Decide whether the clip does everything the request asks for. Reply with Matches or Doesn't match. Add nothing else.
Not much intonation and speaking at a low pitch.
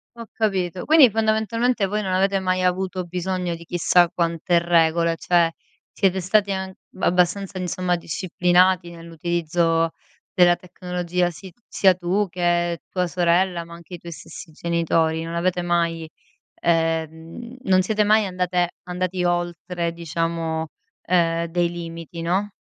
Doesn't match